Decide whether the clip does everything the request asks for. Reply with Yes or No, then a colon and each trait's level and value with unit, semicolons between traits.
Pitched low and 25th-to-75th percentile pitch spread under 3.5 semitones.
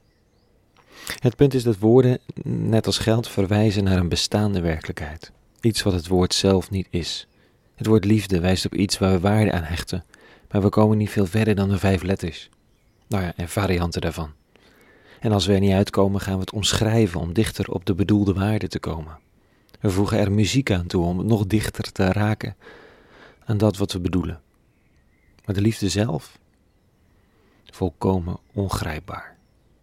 Yes: low, 100 Hz; average, 2.8 semitones